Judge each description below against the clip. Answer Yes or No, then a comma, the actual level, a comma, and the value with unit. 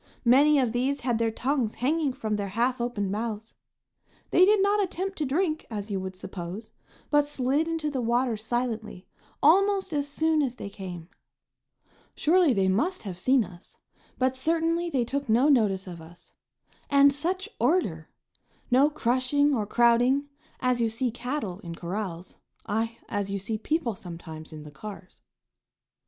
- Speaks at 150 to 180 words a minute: Yes, average, 160 wpm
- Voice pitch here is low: No, high, 245 Hz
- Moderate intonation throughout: No, wide, 6.1 semitones